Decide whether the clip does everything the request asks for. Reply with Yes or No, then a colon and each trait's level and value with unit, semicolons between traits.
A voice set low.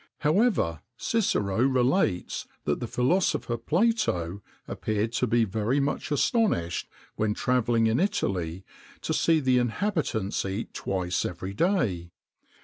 Yes: low, 115 Hz